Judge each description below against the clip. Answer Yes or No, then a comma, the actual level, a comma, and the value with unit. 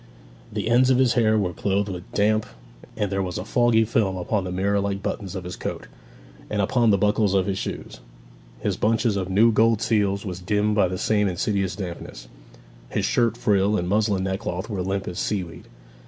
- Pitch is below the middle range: Yes, low, 100 Hz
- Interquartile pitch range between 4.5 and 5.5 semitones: No, narrow, 2.4 semitones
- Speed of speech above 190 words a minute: Yes, average, 200 wpm